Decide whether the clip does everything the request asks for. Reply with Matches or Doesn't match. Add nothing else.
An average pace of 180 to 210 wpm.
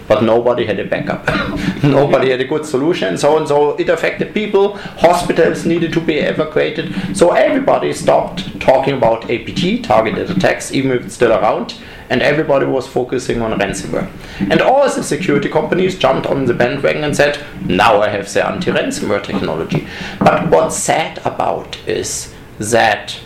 Doesn't match